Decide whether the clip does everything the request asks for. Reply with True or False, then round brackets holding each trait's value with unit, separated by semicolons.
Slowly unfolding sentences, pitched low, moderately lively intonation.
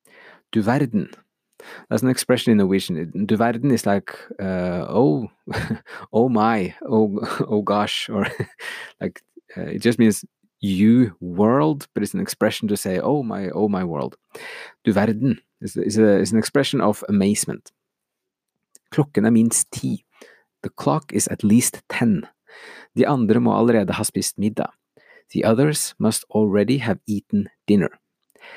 True (130 wpm; 110 Hz; 3.3 semitones)